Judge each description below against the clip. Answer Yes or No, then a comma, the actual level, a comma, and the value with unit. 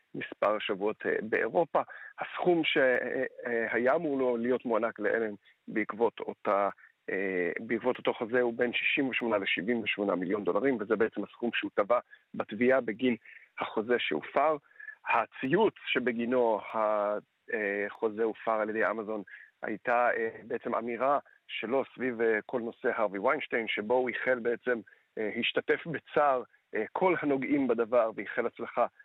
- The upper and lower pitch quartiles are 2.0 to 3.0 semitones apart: Yes, average, 2.7 semitones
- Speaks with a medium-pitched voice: No, low, 120 Hz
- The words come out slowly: No, average, 120 wpm